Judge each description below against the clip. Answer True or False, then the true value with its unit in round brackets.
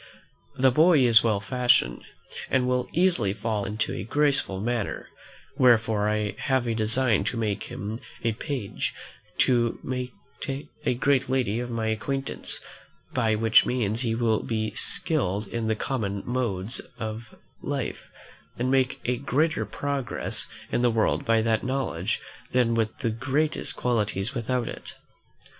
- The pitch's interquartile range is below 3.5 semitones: True (2.9 semitones)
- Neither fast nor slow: True (145 wpm)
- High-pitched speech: False (115 Hz)